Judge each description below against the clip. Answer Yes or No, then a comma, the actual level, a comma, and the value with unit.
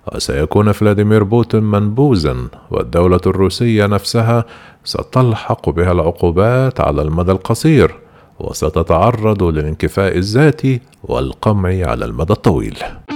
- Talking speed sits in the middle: Yes, average, 90 wpm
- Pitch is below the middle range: Yes, low, 100 Hz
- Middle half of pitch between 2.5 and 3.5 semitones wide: No, average, 4.9 semitones